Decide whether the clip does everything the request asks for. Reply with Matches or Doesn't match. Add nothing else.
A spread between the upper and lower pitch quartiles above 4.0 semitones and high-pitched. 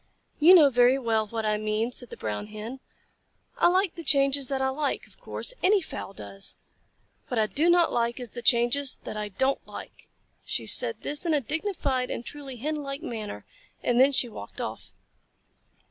Matches